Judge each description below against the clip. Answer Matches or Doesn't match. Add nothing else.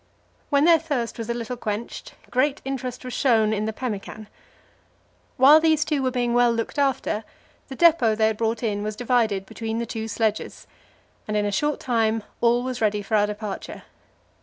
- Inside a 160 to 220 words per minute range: Matches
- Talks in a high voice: Matches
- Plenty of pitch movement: Doesn't match